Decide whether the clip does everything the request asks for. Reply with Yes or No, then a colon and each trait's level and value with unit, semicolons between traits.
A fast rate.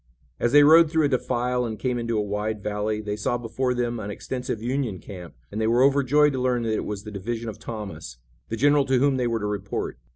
Yes: fast, 240 wpm